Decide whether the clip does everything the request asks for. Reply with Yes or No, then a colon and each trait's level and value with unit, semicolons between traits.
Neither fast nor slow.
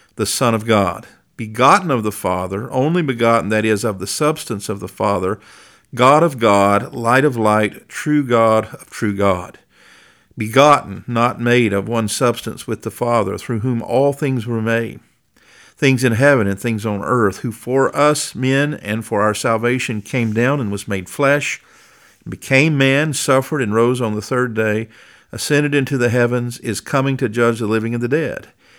Yes: average, 180 wpm